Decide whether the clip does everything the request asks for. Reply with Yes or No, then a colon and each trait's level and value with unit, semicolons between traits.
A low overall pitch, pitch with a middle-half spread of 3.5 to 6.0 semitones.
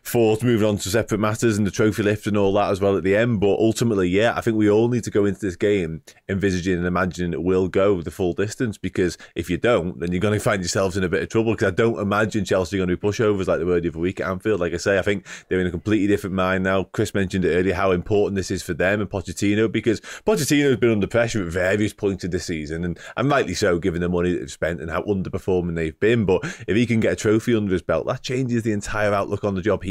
No: low, 100 Hz; average, 2.8 semitones